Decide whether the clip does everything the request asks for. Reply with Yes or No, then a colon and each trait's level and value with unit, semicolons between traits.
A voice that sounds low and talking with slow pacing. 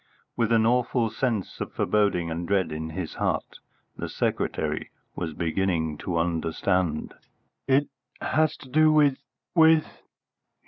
Yes: low, 100 Hz; slow, 130 wpm